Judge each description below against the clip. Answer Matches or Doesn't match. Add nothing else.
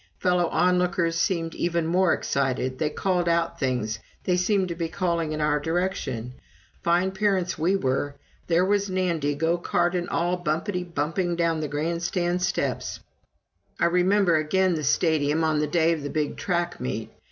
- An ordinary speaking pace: Matches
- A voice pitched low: Doesn't match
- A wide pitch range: Doesn't match